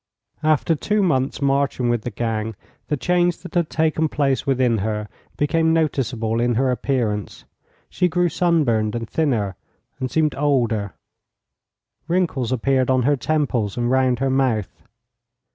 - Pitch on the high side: No, low, 130 Hz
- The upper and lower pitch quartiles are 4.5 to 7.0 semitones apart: Yes, average, 5.0 semitones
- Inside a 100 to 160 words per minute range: Yes, average, 145 wpm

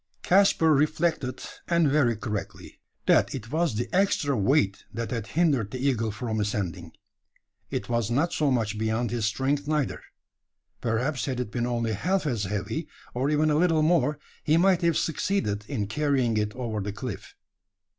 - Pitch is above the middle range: No, low, 125 Hz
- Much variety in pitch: Yes, wide, 5.8 semitones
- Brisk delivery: No, average, 165 wpm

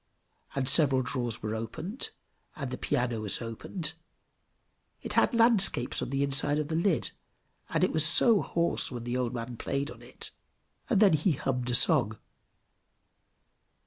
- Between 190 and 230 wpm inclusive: No, average, 160 wpm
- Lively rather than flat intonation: No, average, 4.8 semitones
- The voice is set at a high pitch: No, low, 135 Hz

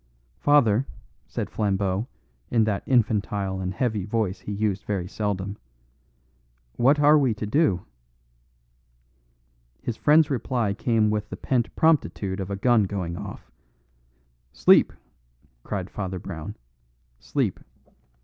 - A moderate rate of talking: No, slow, 120 wpm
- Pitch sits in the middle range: No, low, 105 Hz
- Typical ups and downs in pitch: Yes, average, 3.8 semitones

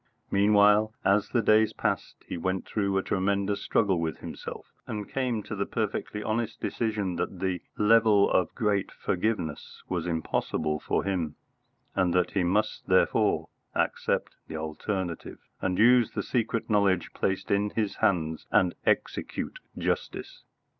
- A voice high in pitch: No, low, 100 Hz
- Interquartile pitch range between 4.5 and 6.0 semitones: No, average, 2.9 semitones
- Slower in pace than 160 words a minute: Yes, average, 145 wpm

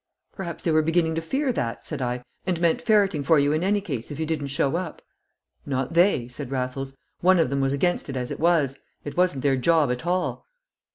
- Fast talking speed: Yes, fast, 225 wpm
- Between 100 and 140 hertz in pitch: No, medium, 155 Hz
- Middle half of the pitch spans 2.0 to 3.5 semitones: No, average, 4.3 semitones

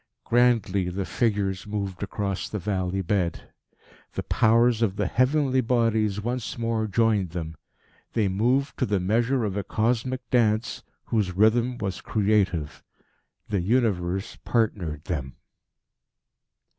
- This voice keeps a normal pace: No, slow, 125 wpm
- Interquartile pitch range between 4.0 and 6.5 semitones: No, average, 3.6 semitones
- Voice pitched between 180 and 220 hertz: No, low, 105 Hz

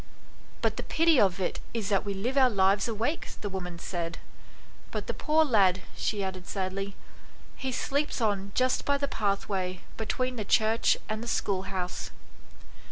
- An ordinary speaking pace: Yes, average, 165 wpm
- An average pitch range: Yes, average, 4.7 semitones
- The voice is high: Yes, high, 205 Hz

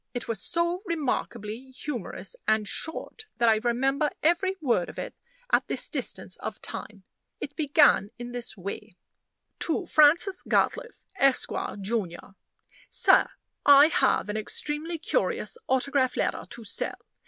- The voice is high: Yes, very high, 270 Hz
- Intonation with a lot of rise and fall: Yes, wide, 5.7 semitones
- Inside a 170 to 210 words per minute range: No, slow, 135 wpm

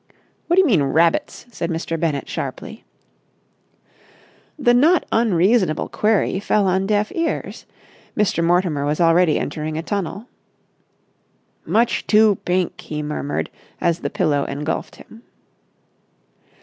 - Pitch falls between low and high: Yes, medium, 180 Hz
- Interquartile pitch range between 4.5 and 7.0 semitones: Yes, average, 5.2 semitones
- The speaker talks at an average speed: No, slow, 125 wpm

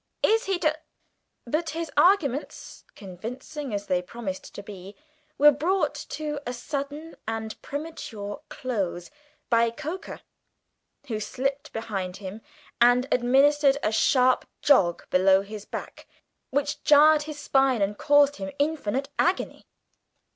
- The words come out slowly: Yes, slow, 130 wpm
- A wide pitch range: Yes, wide, 5.7 semitones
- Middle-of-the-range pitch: No, very high, 265 Hz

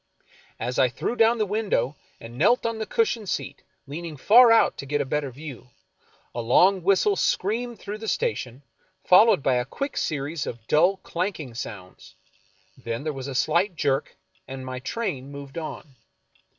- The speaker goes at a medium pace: Yes, average, 175 wpm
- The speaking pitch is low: No, medium, 155 Hz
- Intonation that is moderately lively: No, wide, 8.2 semitones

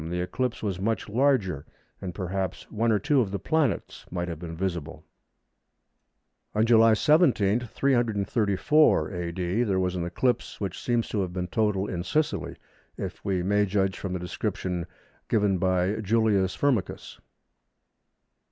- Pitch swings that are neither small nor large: Yes, average, 3.9 semitones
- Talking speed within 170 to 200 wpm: No, average, 145 wpm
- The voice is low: Yes, low, 100 Hz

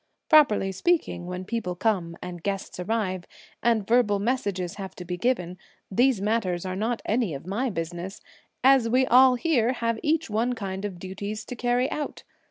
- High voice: Yes, high, 210 Hz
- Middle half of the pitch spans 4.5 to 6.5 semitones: Yes, average, 4.8 semitones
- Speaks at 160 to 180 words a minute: Yes, average, 175 wpm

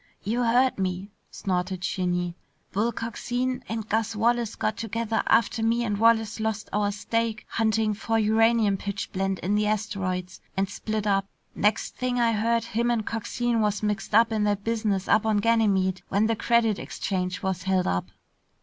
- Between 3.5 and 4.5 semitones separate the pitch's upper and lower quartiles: No, narrow, 2.5 semitones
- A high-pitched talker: Yes, high, 215 Hz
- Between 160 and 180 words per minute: Yes, average, 165 wpm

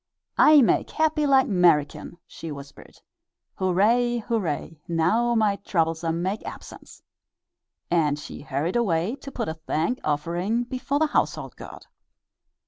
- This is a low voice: No, medium, 185 Hz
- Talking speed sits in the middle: No, slow, 130 wpm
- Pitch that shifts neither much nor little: No, wide, 6.7 semitones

